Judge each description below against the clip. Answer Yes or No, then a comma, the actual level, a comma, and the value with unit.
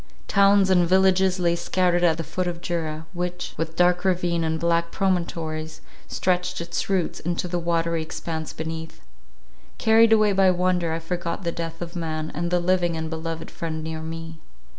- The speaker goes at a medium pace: Yes, average, 175 wpm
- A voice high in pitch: No, medium, 170 Hz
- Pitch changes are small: Yes, narrow, 1.8 semitones